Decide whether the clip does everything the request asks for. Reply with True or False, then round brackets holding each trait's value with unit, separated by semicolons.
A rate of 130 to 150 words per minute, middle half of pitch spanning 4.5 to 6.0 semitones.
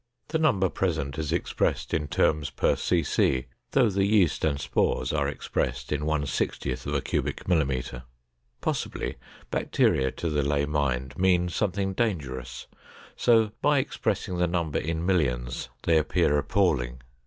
True (140 wpm; 5.3 semitones)